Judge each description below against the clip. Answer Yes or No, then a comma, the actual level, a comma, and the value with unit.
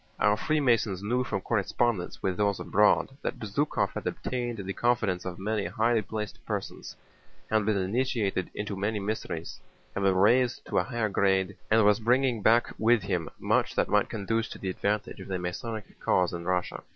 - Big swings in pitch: No, average, 3.2 semitones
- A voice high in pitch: No, low, 105 Hz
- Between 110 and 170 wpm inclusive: No, average, 180 wpm